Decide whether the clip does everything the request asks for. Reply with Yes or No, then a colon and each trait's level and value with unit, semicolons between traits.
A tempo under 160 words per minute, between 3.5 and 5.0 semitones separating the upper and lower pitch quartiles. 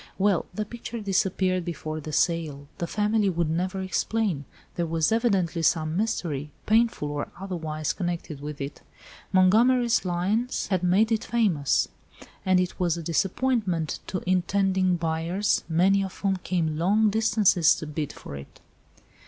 Yes: average, 145 wpm; average, 4.0 semitones